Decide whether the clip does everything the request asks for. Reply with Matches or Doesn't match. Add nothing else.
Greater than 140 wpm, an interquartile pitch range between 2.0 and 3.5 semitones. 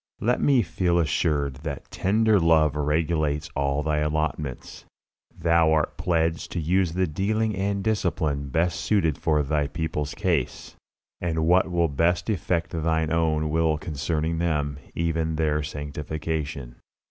Doesn't match